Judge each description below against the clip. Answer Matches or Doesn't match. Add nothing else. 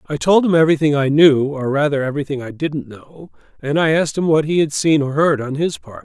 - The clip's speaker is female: Doesn't match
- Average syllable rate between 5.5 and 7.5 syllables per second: Matches